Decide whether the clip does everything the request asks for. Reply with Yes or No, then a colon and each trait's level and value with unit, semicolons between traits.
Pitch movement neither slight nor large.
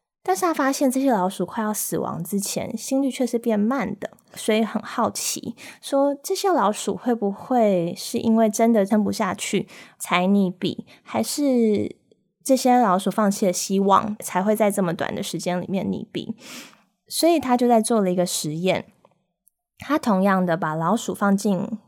Yes: average, 4.1 semitones